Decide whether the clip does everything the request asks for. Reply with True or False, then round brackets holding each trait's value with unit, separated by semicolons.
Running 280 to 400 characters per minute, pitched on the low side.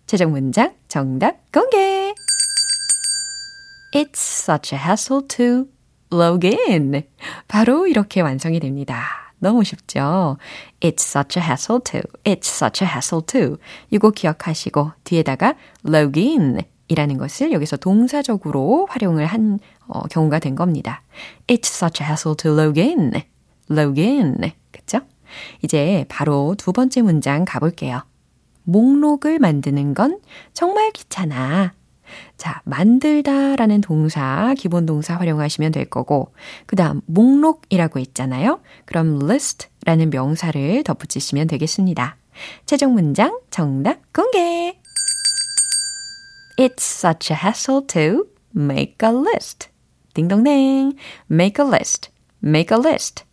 False (310 characters per minute; 185 Hz)